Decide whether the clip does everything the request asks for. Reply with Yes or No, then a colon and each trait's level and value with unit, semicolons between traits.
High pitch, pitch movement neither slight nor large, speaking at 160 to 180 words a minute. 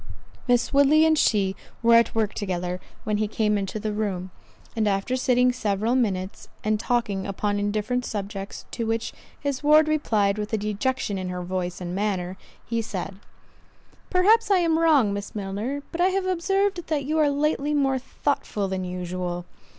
No: high, 215 Hz; wide, 6.3 semitones; average, 170 wpm